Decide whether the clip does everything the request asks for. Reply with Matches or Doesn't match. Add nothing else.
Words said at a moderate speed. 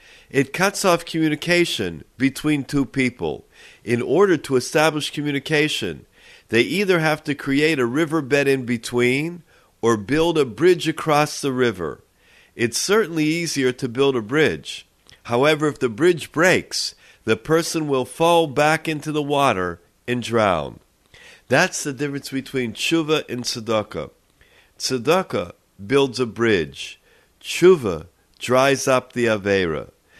Doesn't match